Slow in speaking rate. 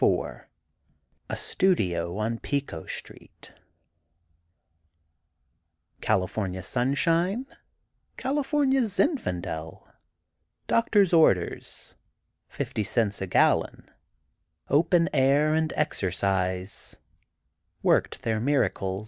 Yes: slow, 65 wpm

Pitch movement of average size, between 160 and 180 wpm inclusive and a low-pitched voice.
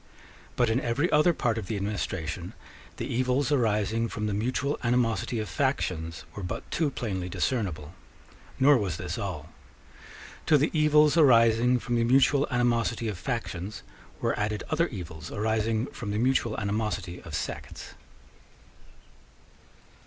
No: average, 3.9 semitones; average, 140 wpm; low, 115 Hz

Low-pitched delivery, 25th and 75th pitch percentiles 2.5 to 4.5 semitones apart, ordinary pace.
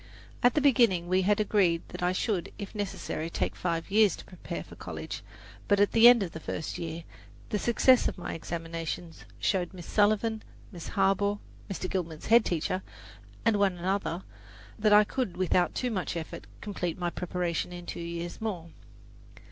No: medium, 185 Hz; average, 3.5 semitones; average, 175 wpm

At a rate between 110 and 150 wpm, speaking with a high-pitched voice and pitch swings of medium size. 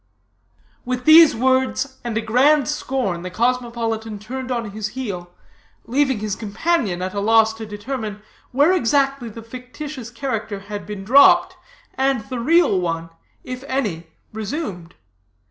Yes: average, 140 wpm; high, 230 Hz; average, 4.1 semitones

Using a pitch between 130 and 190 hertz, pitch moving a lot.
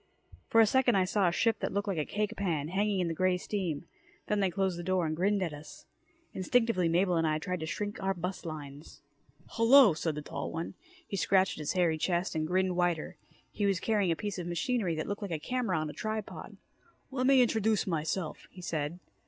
No: medium, 185 Hz; average, 3.8 semitones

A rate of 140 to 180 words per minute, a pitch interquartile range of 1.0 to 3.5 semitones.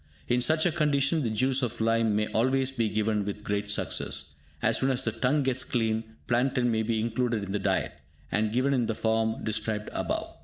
No: fast, 205 wpm; average, 3.1 semitones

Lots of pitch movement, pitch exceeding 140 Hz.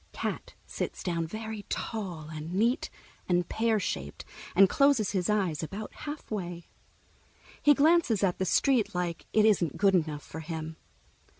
No: average, 4.6 semitones; high, 190 Hz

